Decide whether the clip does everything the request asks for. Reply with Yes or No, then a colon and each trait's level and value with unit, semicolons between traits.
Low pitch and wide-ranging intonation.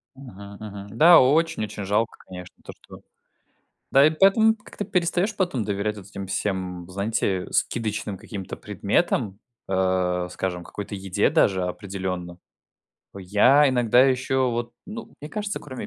Yes: low, 105 Hz; wide, 6.3 semitones